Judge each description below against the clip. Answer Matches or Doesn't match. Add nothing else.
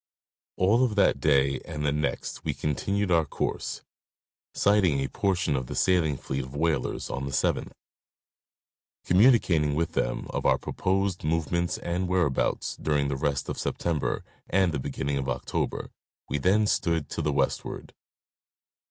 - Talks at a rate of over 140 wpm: Matches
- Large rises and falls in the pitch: Doesn't match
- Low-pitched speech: Matches